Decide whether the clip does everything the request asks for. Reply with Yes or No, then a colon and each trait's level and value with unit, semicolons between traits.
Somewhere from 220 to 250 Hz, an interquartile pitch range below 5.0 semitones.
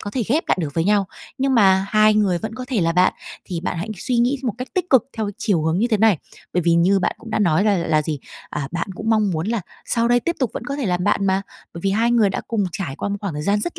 No: high, 205 Hz; average, 4.6 semitones